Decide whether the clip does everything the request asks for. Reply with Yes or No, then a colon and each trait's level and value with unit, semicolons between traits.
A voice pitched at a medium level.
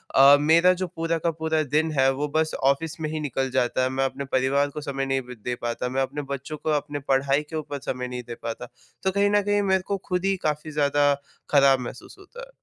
Yes: medium, 145 Hz